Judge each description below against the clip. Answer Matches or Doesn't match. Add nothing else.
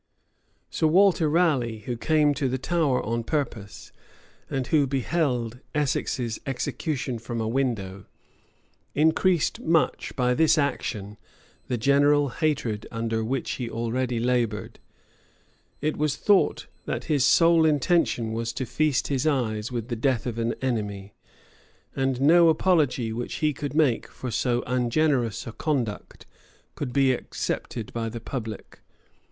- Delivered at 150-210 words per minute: Doesn't match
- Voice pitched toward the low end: Matches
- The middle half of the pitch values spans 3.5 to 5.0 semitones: Matches